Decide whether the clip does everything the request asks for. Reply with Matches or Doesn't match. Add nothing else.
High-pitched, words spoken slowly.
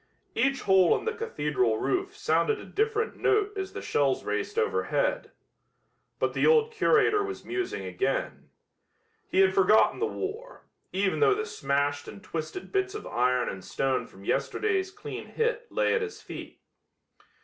Doesn't match